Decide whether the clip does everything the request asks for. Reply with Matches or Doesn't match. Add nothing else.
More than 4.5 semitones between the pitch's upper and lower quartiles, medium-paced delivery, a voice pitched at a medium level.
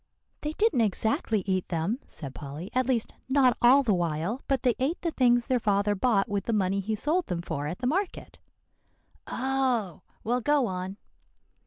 Doesn't match